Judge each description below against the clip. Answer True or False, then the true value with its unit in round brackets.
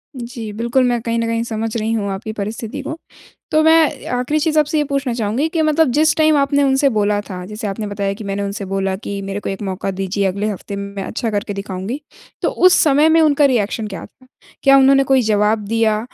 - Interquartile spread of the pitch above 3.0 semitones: True (5.5 semitones)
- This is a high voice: True (225 Hz)